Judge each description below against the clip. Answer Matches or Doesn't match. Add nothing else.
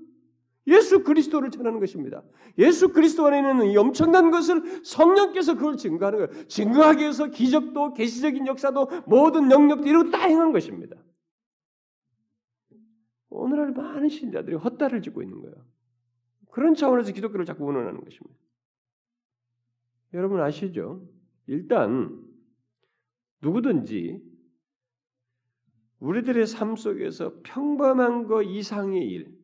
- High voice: Matches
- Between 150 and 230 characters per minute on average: Doesn't match